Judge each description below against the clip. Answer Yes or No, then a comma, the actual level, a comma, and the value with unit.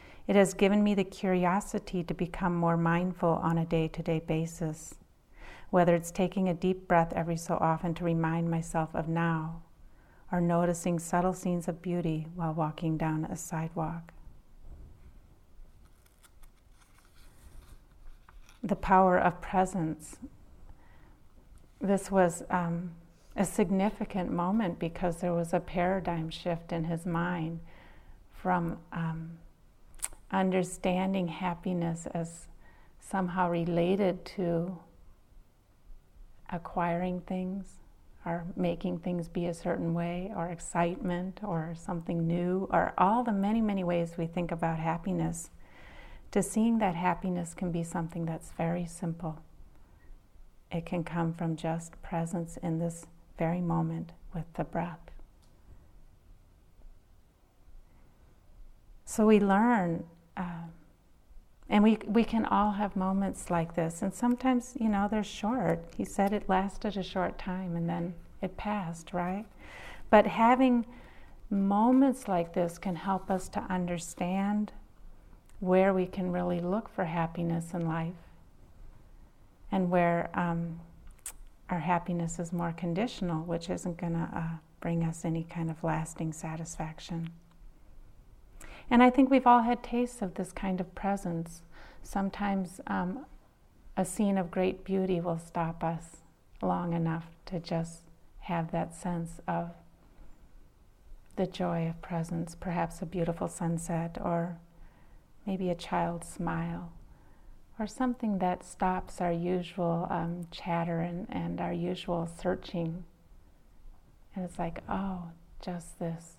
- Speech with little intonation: Yes, narrow, 2.1 semitones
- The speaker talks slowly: Yes, slow, 125 wpm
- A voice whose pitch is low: No, medium, 170 Hz